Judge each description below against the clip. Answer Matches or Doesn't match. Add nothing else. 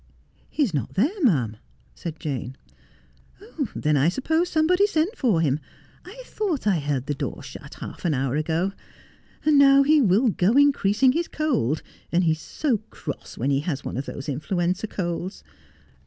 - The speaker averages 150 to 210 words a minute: Matches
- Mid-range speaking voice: Matches